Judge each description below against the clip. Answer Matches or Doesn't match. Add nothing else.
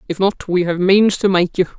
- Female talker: Matches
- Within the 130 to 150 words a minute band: Doesn't match